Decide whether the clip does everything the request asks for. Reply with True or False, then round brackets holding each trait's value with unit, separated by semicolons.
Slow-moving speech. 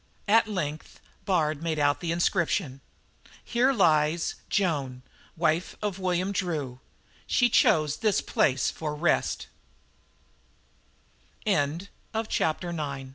True (105 wpm)